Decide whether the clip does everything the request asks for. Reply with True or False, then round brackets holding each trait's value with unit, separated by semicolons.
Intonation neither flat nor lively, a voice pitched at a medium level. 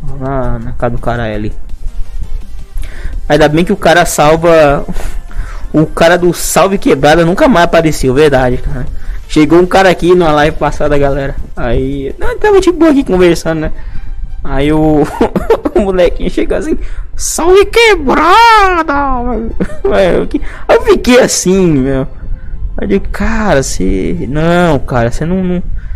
False (7.5 semitones; 155 Hz)